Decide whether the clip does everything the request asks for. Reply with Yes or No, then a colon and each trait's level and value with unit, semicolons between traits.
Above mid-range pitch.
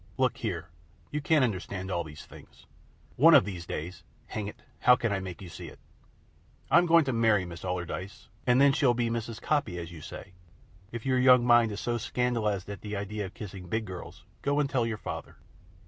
No: low, 110 Hz